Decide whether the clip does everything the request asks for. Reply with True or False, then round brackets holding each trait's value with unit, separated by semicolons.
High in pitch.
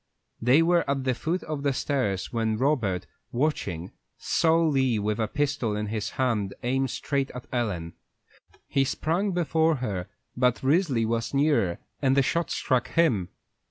False (130 Hz)